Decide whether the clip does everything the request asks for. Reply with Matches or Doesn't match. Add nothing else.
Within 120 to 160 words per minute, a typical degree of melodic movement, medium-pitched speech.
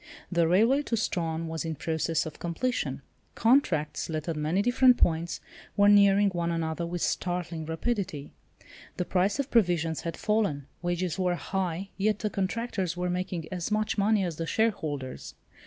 Matches